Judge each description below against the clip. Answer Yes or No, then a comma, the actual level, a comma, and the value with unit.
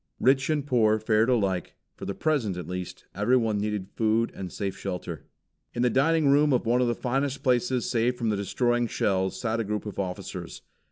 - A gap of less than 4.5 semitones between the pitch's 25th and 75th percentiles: Yes, average, 3.9 semitones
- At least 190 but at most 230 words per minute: Yes, average, 200 wpm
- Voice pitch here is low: Yes, low, 115 Hz